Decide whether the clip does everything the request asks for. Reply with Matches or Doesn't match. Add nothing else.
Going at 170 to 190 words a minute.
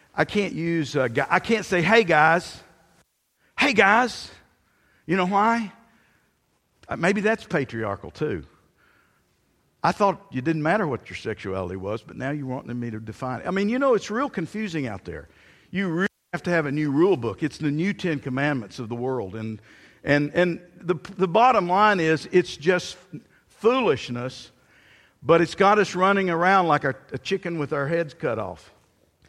Matches